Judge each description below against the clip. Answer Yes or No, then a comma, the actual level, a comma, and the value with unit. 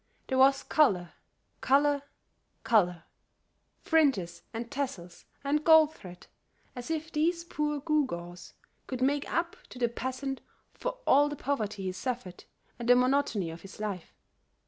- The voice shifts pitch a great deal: Yes, wide, 6.9 semitones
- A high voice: Yes, very high, 260 Hz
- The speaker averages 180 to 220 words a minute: No, average, 140 wpm